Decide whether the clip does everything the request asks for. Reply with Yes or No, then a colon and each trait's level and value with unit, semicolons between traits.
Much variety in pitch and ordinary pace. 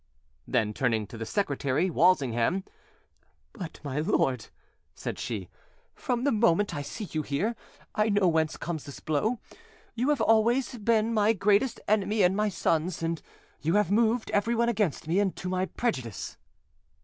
Yes: wide, 6.2 semitones; average, 160 wpm